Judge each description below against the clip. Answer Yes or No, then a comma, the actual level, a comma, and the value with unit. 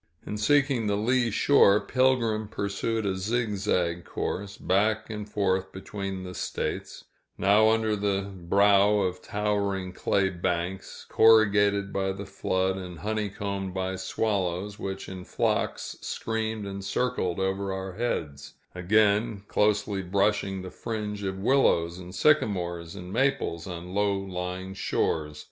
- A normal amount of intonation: No, narrow, 2.3 semitones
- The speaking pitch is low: Yes, low, 100 Hz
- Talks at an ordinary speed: No, slow, 130 wpm